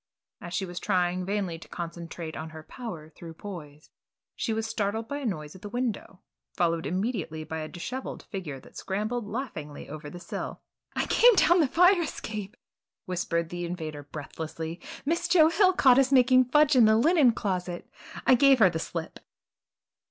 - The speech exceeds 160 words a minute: Yes, average, 180 wpm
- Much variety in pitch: Yes, wide, 7.3 semitones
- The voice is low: No, high, 190 Hz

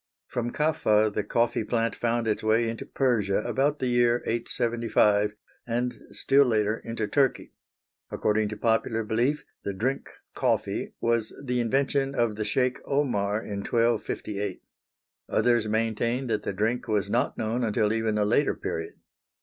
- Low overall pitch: Yes, low, 115 Hz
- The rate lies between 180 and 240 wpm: No, average, 150 wpm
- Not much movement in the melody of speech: Yes, narrow, 2.3 semitones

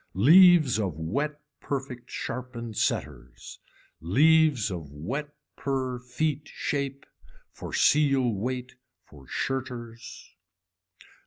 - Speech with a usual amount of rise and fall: Yes, average, 4.3 semitones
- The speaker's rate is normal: No, slow, 90 wpm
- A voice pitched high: No, low, 130 Hz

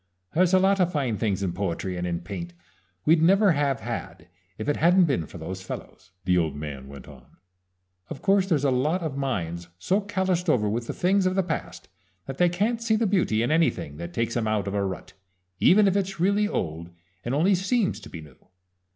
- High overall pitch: No, low, 135 Hz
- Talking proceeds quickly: Yes, fast, 220 wpm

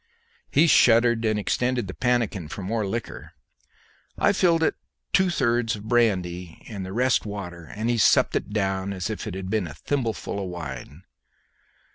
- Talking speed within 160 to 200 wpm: Yes, average, 175 wpm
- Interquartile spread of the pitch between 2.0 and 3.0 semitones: No, average, 4.2 semitones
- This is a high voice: No, low, 105 Hz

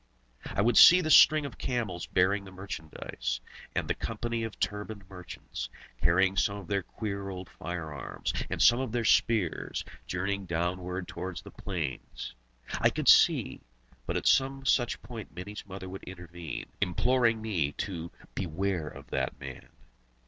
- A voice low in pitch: Yes, very low, 95 Hz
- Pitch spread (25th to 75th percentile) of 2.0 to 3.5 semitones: No, average, 4.1 semitones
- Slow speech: No, average, 155 wpm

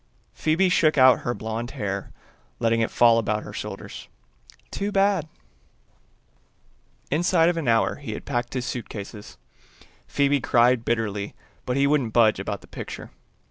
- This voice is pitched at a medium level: No, low, 120 Hz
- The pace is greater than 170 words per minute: No, average, 140 wpm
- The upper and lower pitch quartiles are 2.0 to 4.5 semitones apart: No, average, 4.9 semitones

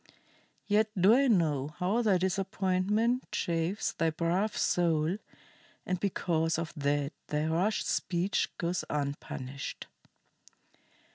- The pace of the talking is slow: Yes, slow, 110 wpm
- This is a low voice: No, medium, 175 Hz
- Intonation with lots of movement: No, average, 3.9 semitones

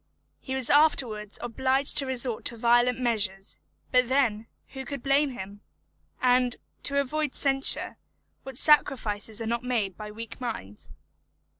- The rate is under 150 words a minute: Yes, average, 140 wpm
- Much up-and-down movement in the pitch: No, average, 3.4 semitones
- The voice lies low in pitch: No, high, 245 Hz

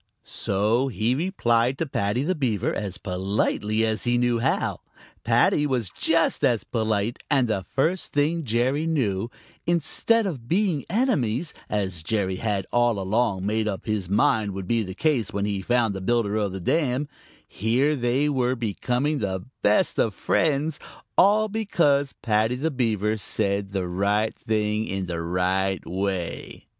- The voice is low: Yes, low, 115 Hz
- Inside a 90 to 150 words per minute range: No, average, 160 wpm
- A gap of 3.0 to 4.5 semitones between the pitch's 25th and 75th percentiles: No, wide, 5.5 semitones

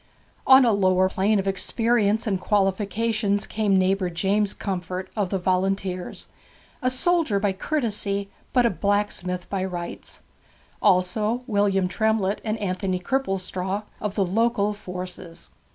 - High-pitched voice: Yes, high, 200 Hz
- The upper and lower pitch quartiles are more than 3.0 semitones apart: No, narrow, 2.5 semitones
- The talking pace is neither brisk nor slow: No, slow, 130 wpm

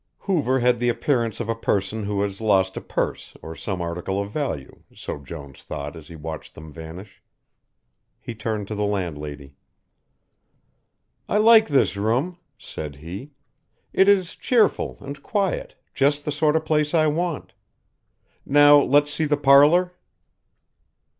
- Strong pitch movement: Yes, wide, 8.2 semitones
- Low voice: Yes, low, 115 Hz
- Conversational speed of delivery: Yes, average, 150 wpm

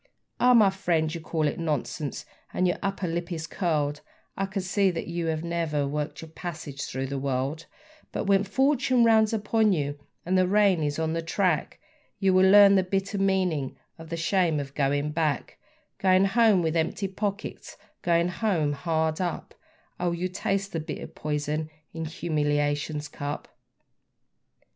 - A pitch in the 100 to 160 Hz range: No, medium, 170 Hz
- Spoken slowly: No, average, 165 wpm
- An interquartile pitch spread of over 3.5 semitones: Yes, average, 4.2 semitones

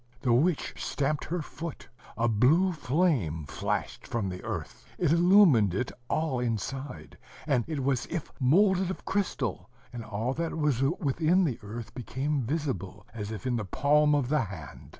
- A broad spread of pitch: Yes, wide, 5.7 semitones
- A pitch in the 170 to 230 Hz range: No, low, 135 Hz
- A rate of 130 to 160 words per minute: No, average, 170 wpm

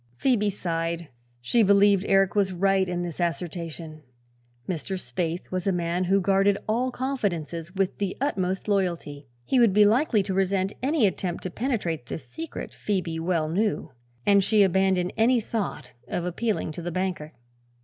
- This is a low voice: No, high, 190 Hz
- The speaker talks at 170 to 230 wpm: No, average, 160 wpm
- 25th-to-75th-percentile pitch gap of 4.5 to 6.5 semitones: No, average, 3.1 semitones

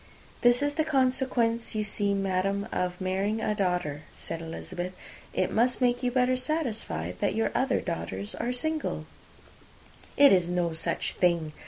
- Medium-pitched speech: No, high, 205 Hz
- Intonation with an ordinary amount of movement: No, wide, 5.9 semitones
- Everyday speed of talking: Yes, average, 155 wpm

